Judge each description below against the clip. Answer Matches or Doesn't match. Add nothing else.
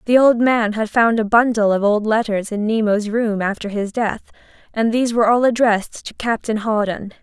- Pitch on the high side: Matches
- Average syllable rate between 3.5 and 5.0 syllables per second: Doesn't match